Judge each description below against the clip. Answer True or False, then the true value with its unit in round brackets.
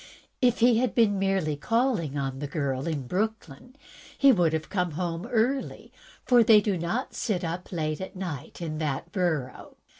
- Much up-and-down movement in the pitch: True (6.3 semitones)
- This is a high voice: False (180 Hz)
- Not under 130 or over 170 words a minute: True (160 wpm)